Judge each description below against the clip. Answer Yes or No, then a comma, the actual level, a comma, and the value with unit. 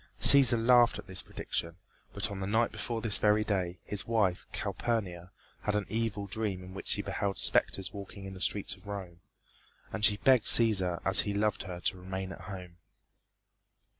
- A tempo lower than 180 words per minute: No, average, 185 wpm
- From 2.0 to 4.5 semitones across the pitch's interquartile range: Yes, average, 2.8 semitones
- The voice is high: No, low, 100 Hz